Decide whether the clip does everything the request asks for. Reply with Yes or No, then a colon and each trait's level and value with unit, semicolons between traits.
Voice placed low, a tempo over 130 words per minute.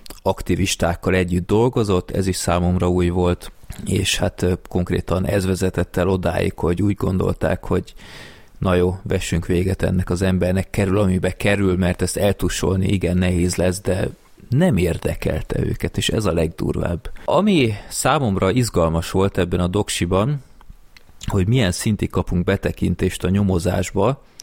Yes: very low, 95 Hz; average, 140 wpm